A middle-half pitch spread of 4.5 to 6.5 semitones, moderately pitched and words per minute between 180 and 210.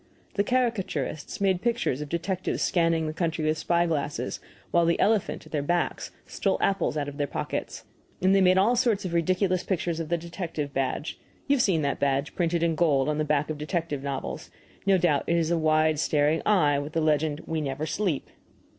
No: average, 3.6 semitones; medium, 165 Hz; fast, 205 wpm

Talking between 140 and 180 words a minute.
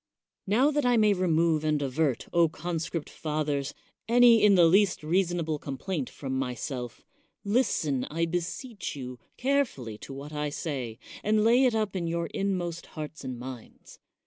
Yes: average, 160 wpm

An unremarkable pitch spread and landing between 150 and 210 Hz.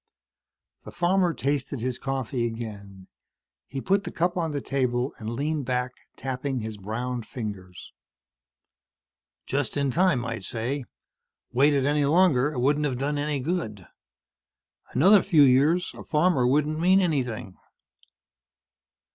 No: average, 3.8 semitones; low, 135 Hz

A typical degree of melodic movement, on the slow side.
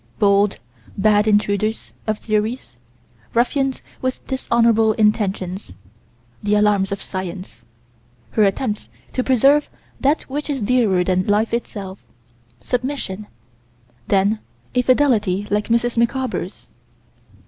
Yes: average, 3.7 semitones; slow, 105 wpm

